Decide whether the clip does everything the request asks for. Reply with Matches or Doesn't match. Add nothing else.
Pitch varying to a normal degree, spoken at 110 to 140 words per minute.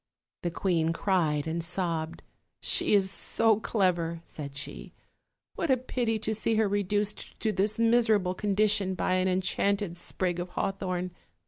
Doesn't match